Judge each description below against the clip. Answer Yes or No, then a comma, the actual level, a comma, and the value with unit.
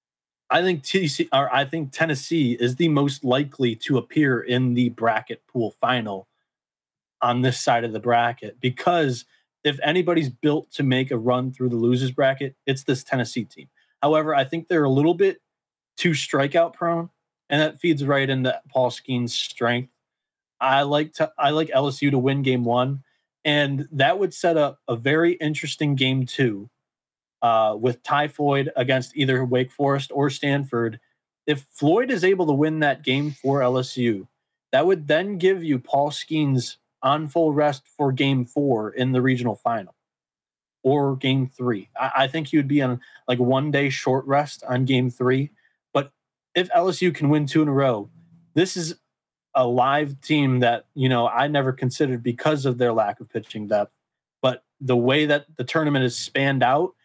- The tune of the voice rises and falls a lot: No, average, 3.2 semitones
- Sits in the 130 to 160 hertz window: Yes, low, 135 Hz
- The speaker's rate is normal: Yes, average, 180 wpm